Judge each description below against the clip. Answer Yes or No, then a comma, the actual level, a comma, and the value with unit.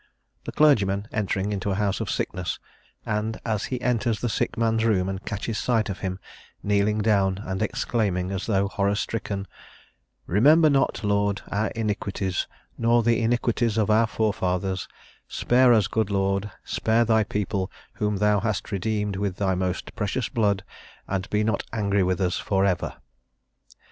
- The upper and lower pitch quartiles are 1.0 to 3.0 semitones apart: Yes, narrow, 2.4 semitones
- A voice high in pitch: No, low, 105 Hz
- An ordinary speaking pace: Yes, average, 160 wpm